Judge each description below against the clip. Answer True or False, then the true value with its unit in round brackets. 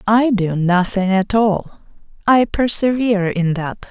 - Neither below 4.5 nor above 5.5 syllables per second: False (4.1 syllables/s)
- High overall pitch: True (205 Hz)